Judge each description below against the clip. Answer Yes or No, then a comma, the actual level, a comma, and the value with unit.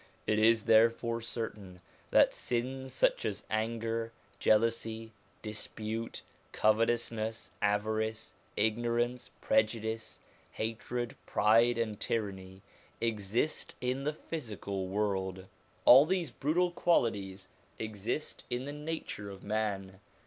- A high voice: No, low, 115 Hz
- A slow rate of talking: Yes, slow, 100 wpm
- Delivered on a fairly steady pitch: Yes, narrow, 2.2 semitones